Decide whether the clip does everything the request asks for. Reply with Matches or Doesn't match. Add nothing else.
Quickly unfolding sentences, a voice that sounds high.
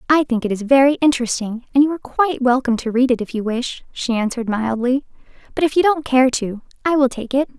Matches